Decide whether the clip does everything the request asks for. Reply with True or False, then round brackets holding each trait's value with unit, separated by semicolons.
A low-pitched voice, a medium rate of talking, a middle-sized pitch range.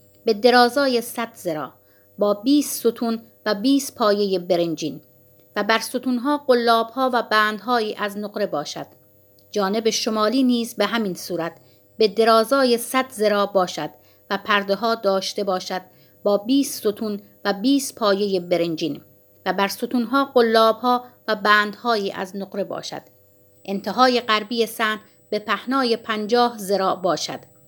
False (215 Hz; 130 wpm; 3.7 semitones)